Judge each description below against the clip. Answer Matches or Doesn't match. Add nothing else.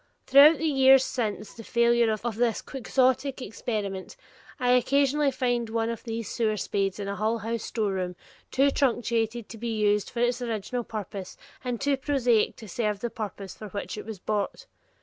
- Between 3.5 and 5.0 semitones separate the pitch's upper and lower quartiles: Doesn't match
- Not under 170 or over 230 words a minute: Matches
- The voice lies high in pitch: Matches